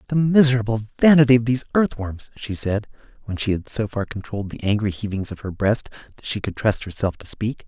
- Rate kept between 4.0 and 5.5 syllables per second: No, 6.0 syllables/s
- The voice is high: No, low, 110 Hz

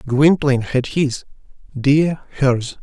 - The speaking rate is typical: No, slow, 105 wpm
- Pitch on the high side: No, medium, 140 Hz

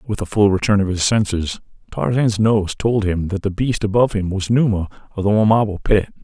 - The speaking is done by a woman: No, male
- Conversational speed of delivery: No, fast, 210 wpm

